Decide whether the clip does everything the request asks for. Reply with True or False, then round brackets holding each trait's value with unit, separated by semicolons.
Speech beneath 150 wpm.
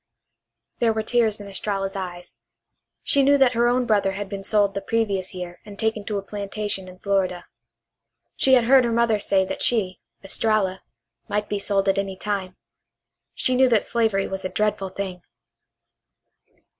False (170 wpm)